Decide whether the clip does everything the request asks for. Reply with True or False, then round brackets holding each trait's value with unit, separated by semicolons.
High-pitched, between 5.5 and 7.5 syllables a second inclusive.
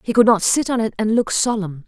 True (215 Hz; 5.8 syllables/s)